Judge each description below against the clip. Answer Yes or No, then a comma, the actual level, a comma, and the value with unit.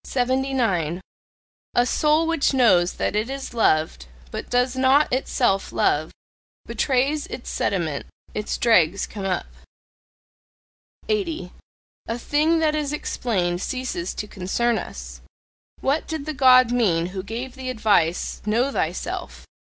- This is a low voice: No, high, 245 Hz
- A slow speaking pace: Yes, slow, 125 wpm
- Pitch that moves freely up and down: Yes, wide, 6.4 semitones